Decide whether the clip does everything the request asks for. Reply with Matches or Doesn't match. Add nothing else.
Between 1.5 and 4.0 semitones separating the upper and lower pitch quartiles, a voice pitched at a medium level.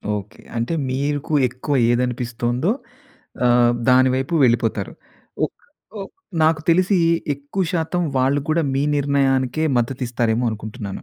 Doesn't match